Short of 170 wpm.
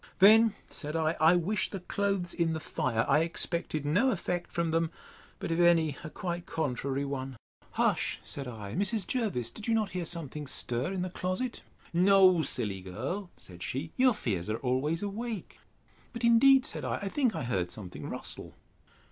No: average, 175 wpm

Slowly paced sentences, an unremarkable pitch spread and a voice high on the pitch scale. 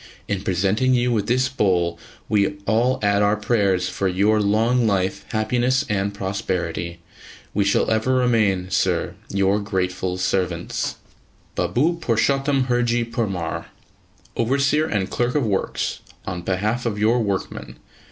No: slow, 130 wpm; average, 4.2 semitones; low, 105 Hz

